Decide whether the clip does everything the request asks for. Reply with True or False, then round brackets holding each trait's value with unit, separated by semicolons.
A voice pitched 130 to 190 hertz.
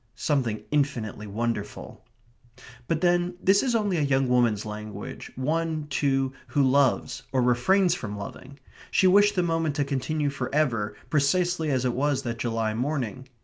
True (140 Hz)